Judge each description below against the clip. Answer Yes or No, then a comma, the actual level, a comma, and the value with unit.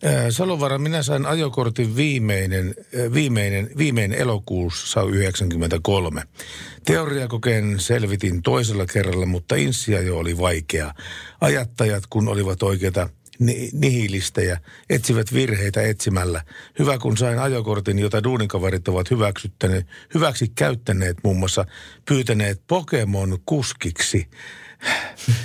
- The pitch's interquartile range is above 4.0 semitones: Yes, average, 4.7 semitones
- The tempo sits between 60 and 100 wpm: Yes, slow, 95 wpm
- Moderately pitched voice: No, low, 105 Hz